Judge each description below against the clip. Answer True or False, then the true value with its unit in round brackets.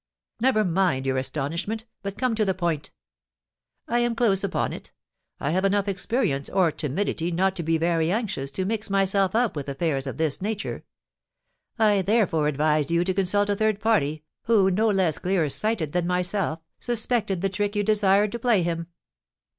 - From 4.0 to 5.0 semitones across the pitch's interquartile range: True (4.3 semitones)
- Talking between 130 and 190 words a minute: True (180 wpm)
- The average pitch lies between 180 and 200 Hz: True (190 Hz)